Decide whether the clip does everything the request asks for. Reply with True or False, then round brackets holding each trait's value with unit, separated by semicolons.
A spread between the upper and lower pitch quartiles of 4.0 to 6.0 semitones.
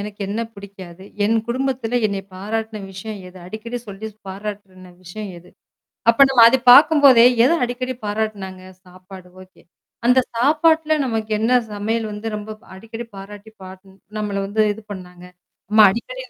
False (3.4 semitones)